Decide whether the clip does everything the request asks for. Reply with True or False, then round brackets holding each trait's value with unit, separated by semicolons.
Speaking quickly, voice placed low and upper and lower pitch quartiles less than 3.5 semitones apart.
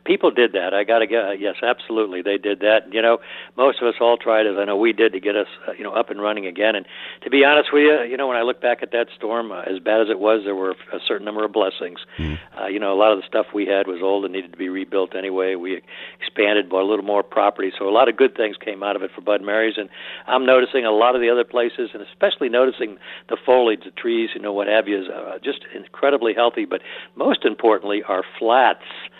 True (275 wpm; 110 Hz; 2.8 semitones)